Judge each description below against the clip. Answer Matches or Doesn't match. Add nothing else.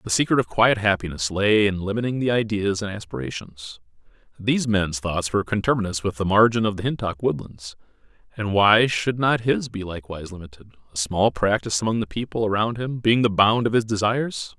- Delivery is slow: Doesn't match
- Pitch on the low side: Matches